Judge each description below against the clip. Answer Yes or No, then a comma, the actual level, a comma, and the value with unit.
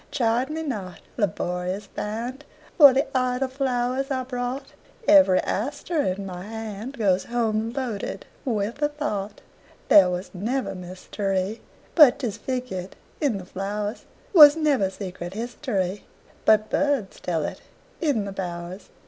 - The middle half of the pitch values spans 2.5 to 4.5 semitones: No, wide, 5.6 semitones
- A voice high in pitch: Yes, high, 225 Hz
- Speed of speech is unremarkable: No, slow, 115 wpm